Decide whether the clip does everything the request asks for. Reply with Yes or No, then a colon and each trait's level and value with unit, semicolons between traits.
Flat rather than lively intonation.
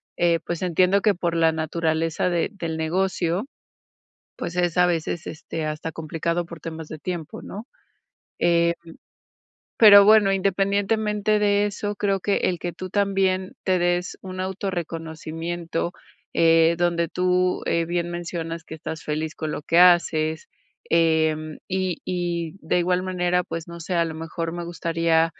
Yes: narrow, 2.3 semitones